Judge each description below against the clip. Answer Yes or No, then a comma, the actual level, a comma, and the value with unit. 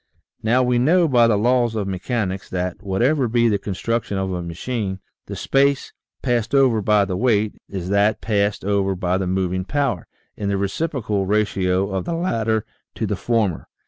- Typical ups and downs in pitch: Yes, average, 4.0 semitones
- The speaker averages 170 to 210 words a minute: Yes, average, 180 wpm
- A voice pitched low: Yes, low, 105 Hz